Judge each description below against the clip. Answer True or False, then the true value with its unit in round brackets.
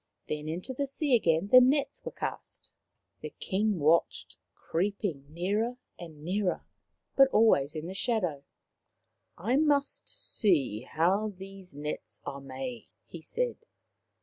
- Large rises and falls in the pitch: True (6.5 semitones)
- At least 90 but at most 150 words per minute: True (135 wpm)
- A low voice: False (185 Hz)